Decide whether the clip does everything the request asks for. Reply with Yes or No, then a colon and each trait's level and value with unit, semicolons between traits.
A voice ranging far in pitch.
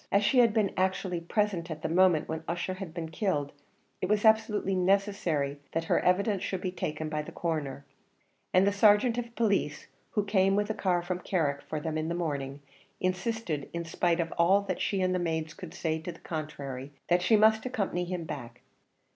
No: average, 4.0 semitones